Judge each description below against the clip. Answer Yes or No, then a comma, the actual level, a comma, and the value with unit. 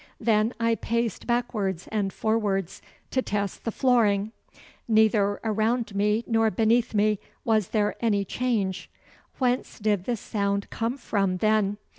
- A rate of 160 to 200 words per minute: No, slow, 135 wpm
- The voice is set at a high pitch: Yes, high, 215 Hz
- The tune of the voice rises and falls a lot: No, narrow, 2.4 semitones